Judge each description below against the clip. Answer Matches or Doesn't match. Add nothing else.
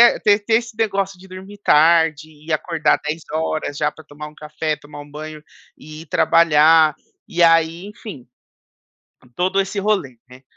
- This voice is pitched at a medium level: Matches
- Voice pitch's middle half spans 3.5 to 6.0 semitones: Matches